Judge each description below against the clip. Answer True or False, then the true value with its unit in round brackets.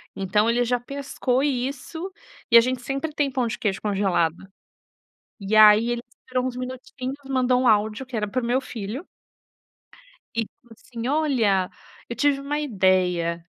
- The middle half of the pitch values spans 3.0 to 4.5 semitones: True (3.9 semitones)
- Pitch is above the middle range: True (245 Hz)